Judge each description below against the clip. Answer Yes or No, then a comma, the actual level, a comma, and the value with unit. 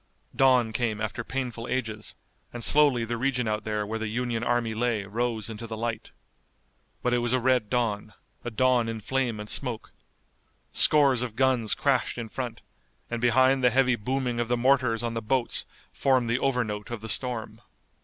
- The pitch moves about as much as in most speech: No, narrow, 2.3 semitones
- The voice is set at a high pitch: No, low, 120 Hz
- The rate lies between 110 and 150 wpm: No, average, 185 wpm